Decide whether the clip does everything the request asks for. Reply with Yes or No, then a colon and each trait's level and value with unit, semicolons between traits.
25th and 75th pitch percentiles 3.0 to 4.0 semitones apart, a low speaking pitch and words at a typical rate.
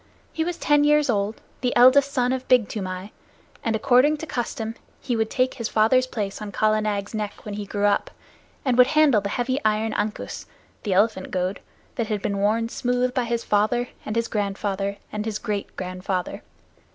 No: average, 3.5 semitones; high, 220 Hz; average, 190 wpm